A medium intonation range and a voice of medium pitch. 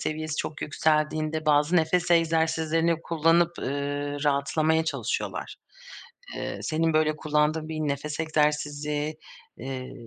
No: narrow, 1.4 semitones; medium, 155 Hz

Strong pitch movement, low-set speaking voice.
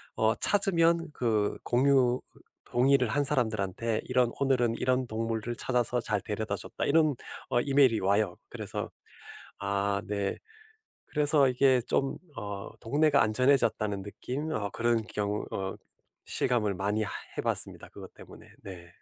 No: average, 4.7 semitones; low, 120 Hz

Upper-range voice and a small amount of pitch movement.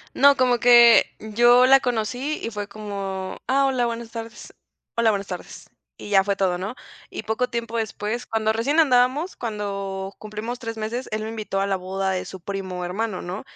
No: high, 220 Hz; average, 3.5 semitones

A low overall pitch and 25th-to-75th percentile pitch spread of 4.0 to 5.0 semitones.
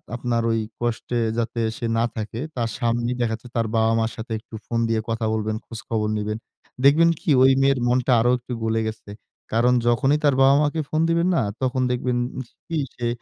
No: low, 120 Hz; narrow, 2.4 semitones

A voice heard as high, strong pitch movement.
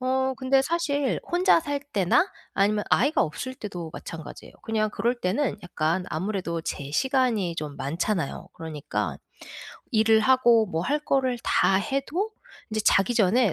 Yes: high, 220 Hz; wide, 6.6 semitones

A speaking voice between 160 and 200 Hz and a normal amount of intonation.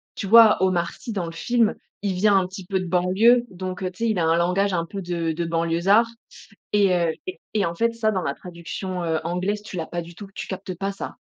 Yes: medium, 185 Hz; average, 3.2 semitones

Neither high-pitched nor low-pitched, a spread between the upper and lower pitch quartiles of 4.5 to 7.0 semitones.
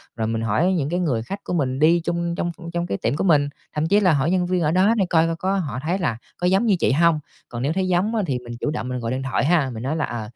Yes: medium, 165 Hz; wide, 5.4 semitones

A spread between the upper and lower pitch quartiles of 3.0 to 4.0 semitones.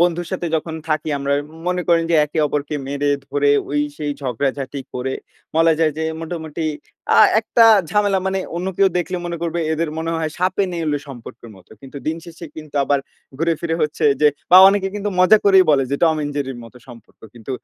Yes: average, 3.4 semitones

